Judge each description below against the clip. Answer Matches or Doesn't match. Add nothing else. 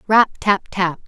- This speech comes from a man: Doesn't match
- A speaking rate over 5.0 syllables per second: Doesn't match